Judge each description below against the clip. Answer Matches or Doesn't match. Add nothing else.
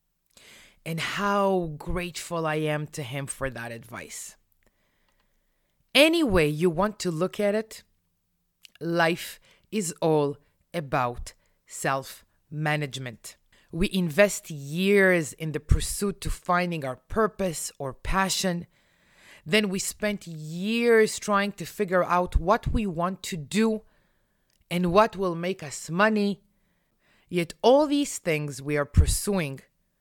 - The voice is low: Doesn't match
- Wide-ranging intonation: Matches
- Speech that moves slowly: Matches